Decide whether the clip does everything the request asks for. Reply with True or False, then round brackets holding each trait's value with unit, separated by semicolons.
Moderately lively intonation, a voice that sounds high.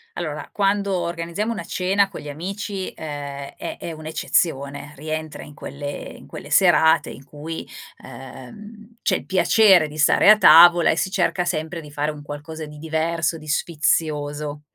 False (3.5 semitones; 160 Hz)